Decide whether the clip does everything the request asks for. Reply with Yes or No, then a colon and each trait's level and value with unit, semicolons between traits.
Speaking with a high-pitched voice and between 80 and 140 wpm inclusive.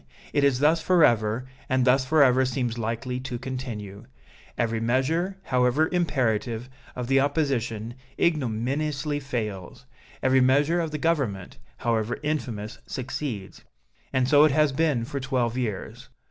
No: low, 130 Hz; slow, 135 wpm